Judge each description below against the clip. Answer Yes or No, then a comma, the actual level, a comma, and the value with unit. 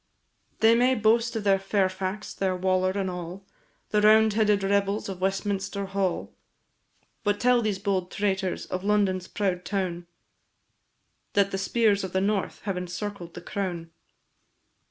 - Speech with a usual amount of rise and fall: No, narrow, 2.0 semitones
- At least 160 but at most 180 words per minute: No, average, 140 wpm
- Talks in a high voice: Yes, high, 195 Hz